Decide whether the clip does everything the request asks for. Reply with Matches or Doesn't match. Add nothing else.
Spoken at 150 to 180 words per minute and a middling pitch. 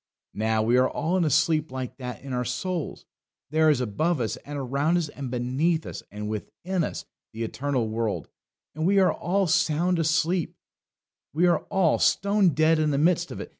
Doesn't match